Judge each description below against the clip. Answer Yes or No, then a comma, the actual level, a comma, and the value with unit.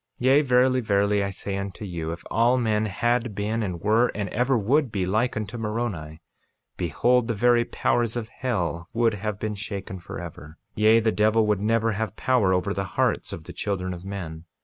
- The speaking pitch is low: Yes, low, 105 Hz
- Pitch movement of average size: Yes, average, 3.4 semitones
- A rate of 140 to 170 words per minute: No, average, 195 wpm